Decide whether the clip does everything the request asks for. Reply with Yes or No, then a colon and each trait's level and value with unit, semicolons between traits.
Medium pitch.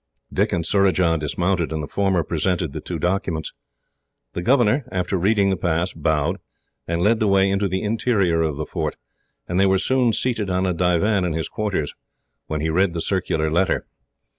No: very low, 90 Hz